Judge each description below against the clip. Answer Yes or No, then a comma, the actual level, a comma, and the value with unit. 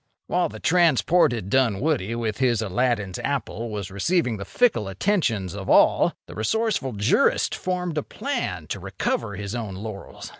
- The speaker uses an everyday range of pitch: No, wide, 6.8 semitones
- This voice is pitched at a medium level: No, low, 115 Hz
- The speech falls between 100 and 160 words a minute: Yes, average, 150 wpm